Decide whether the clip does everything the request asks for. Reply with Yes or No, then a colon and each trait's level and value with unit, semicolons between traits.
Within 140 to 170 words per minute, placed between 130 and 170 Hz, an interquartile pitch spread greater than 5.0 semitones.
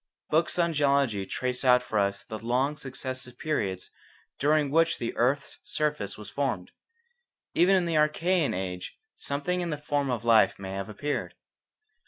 Yes: average, 160 wpm; low, 135 Hz; wide, 5.5 semitones